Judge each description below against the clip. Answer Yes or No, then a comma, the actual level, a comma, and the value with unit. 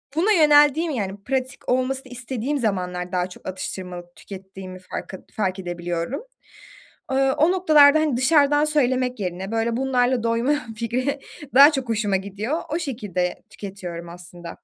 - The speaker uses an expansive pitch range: Yes, wide, 6.7 semitones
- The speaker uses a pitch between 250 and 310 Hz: No, high, 235 Hz